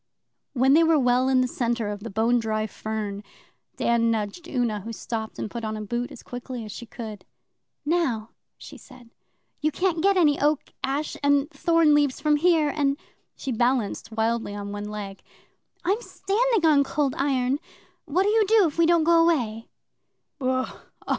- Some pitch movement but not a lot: No, wide, 5.7 semitones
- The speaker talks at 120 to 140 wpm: No, average, 175 wpm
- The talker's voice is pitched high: Yes, very high, 255 Hz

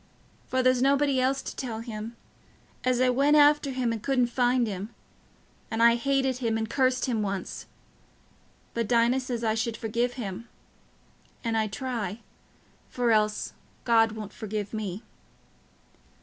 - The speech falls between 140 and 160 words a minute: Yes, average, 150 wpm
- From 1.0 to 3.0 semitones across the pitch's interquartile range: Yes, narrow, 2.6 semitones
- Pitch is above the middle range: Yes, high, 235 Hz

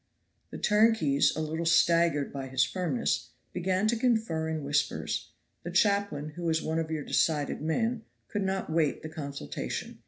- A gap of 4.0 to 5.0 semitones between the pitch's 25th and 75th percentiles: Yes, average, 4.4 semitones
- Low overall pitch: No, medium, 160 Hz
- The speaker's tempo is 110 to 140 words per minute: No, average, 160 wpm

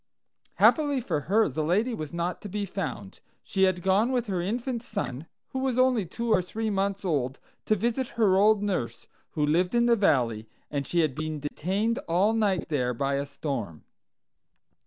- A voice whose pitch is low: No, high, 190 Hz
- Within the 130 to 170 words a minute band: No, average, 185 wpm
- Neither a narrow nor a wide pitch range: No, wide, 6.8 semitones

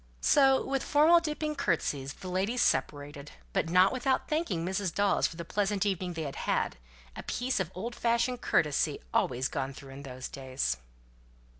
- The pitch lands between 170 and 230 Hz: Yes, medium, 185 Hz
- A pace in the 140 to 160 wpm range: No, average, 170 wpm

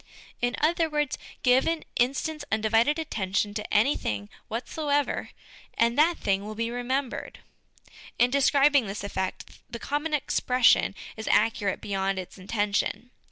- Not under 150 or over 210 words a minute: No, slow, 135 wpm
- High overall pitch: Yes, high, 240 Hz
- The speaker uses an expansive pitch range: Yes, wide, 5.7 semitones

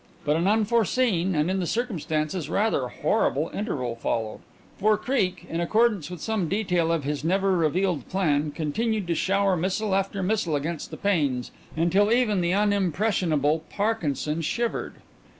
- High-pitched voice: No, medium, 180 Hz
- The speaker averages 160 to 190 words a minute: No, average, 150 wpm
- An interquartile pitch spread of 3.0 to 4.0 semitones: No, average, 4.8 semitones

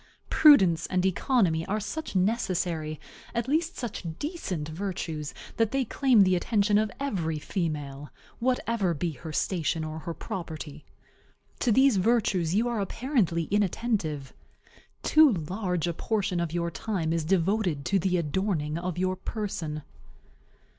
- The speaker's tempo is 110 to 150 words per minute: Yes, average, 140 wpm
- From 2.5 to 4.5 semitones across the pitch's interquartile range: No, average, 5.3 semitones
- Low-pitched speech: No, medium, 185 Hz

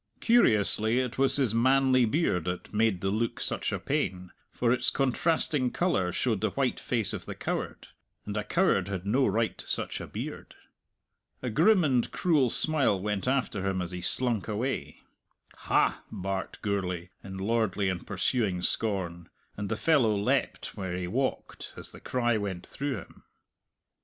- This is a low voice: Yes, low, 110 Hz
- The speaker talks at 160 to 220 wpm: Yes, average, 165 wpm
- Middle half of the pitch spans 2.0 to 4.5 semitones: No, average, 5.2 semitones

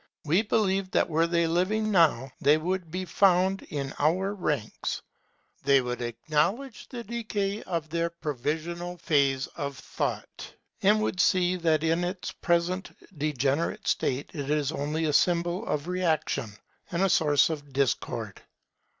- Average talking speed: Yes, average, 145 wpm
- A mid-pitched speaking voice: Yes, medium, 170 Hz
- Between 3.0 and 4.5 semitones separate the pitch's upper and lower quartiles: Yes, average, 4.1 semitones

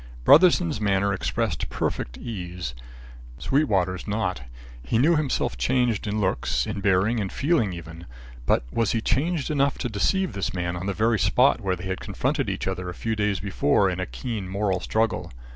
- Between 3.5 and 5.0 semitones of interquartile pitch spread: Yes, average, 4.7 semitones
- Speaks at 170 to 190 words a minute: Yes, average, 175 wpm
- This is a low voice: Yes, low, 100 Hz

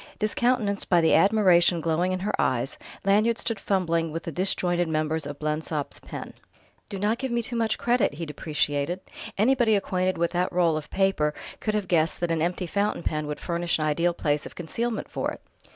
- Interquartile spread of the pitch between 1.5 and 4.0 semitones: No, average, 4.4 semitones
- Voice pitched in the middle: Yes, medium, 175 Hz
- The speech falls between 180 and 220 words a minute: Yes, average, 195 wpm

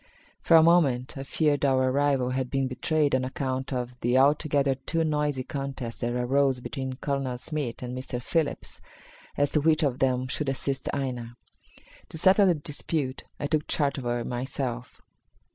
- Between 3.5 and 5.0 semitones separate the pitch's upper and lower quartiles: No, narrow, 2.5 semitones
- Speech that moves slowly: No, average, 170 wpm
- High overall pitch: No, low, 135 Hz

